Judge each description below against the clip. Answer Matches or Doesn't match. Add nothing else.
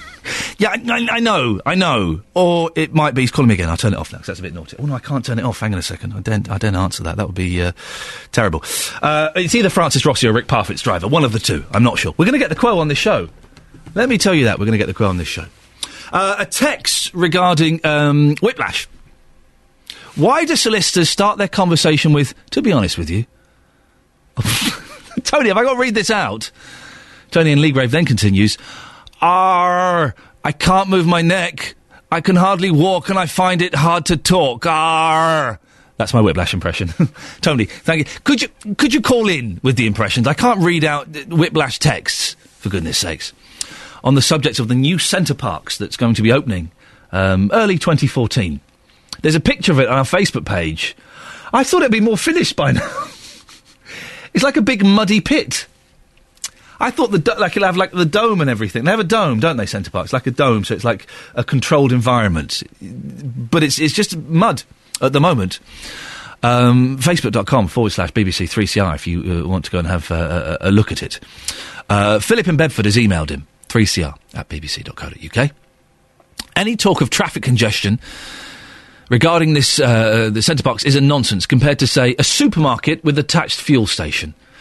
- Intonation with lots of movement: Matches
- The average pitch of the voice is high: Doesn't match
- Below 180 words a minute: Doesn't match